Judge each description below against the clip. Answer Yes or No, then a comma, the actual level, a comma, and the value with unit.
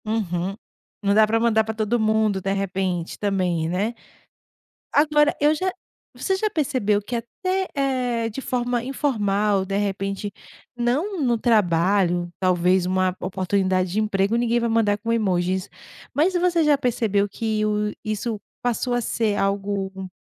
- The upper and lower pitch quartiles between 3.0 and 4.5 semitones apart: Yes, average, 3.8 semitones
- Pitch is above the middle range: Yes, high, 215 Hz